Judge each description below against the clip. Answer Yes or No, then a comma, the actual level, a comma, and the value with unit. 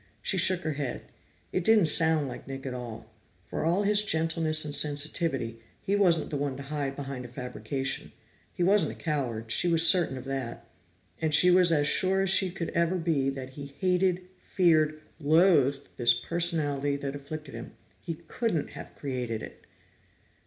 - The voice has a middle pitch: Yes, medium, 155 Hz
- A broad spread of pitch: No, average, 4.2 semitones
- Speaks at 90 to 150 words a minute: No, average, 175 wpm